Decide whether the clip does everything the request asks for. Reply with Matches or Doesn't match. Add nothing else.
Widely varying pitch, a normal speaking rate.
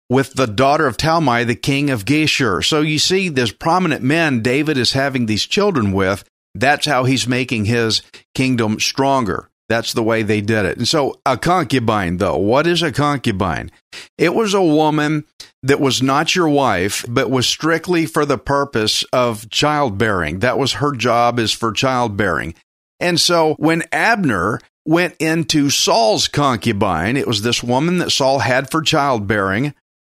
Doesn't match